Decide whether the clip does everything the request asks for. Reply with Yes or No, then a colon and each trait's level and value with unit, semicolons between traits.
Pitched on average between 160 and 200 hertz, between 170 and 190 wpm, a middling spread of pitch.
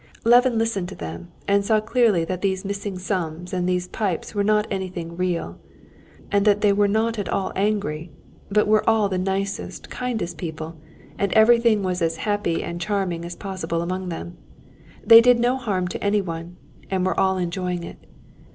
Yes: high, 190 Hz; average, 180 wpm; average, 3.2 semitones